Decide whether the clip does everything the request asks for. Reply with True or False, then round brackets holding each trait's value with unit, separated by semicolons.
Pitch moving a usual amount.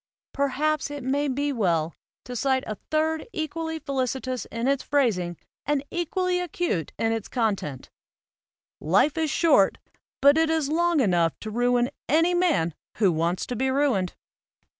False (6.2 semitones)